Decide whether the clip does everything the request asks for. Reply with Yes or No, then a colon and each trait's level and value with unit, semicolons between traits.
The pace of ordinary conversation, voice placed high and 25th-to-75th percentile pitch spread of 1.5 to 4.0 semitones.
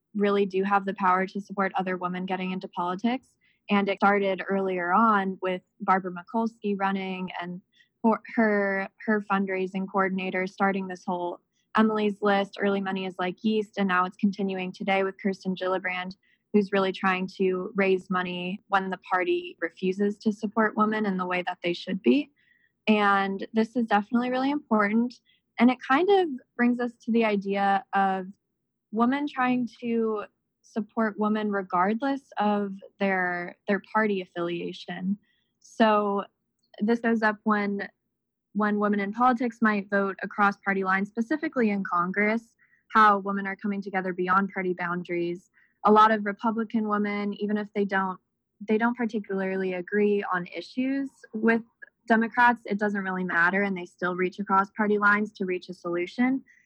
Yes: average, 160 wpm; high, 200 Hz; average, 2.7 semitones